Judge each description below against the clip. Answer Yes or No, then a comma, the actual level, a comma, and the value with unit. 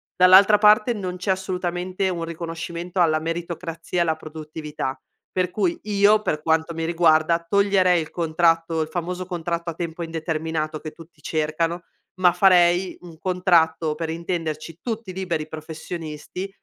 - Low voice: No, medium, 170 Hz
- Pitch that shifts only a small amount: Yes, narrow, 2.2 semitones